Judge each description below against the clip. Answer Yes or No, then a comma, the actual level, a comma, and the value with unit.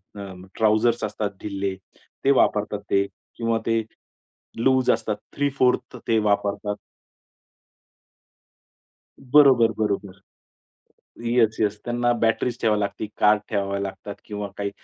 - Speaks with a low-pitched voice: Yes, low, 105 Hz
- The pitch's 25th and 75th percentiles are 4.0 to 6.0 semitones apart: No, average, 2.7 semitones